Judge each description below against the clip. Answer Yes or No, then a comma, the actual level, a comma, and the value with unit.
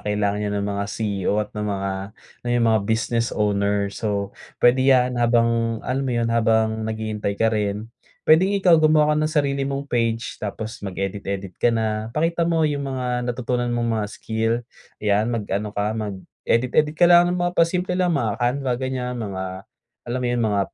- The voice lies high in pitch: No, low, 115 Hz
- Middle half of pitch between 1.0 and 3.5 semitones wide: No, average, 4.1 semitones